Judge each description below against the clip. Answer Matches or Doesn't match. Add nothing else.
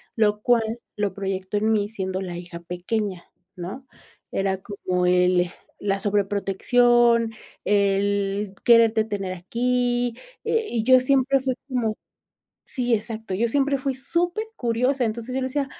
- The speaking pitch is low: Doesn't match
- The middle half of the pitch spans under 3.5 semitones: Doesn't match